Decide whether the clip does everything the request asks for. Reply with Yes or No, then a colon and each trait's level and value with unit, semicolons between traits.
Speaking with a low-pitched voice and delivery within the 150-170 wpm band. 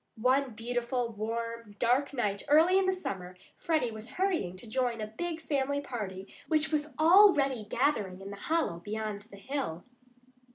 No: high, 245 Hz; average, 160 wpm